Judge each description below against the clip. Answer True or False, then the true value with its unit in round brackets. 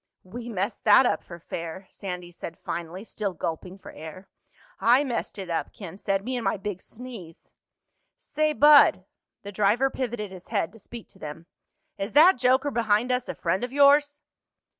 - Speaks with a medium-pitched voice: False (205 Hz)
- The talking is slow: False (170 wpm)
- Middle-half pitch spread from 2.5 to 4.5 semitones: False (5.5 semitones)